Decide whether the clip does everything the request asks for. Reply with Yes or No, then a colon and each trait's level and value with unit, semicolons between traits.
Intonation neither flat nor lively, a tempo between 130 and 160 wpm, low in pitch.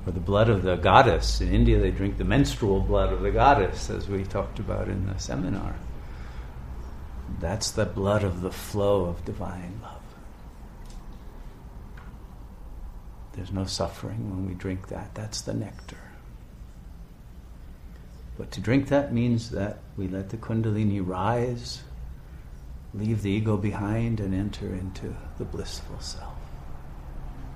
No: wide, 6.5 semitones; average, 140 wpm; very low, 95 Hz